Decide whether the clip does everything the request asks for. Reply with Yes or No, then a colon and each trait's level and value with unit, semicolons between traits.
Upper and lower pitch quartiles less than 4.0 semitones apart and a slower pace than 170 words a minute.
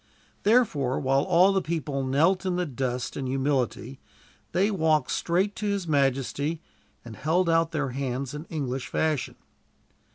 No: average, 4.6 semitones; average, 150 wpm